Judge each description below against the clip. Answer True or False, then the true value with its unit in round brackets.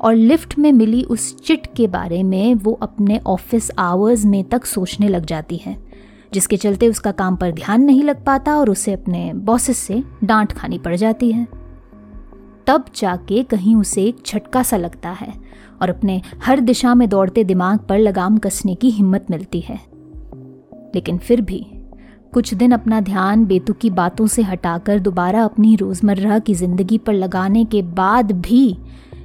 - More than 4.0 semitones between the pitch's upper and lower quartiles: False (3.5 semitones)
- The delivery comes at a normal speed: True (170 wpm)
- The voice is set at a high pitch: True (210 Hz)